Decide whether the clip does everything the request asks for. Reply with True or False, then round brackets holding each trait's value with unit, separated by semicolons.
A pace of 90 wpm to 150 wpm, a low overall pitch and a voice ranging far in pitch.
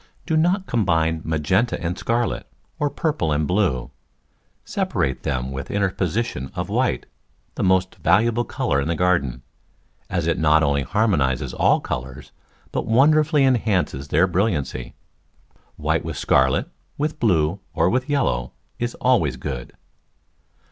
True (140 wpm; 90 Hz; 8.6 semitones)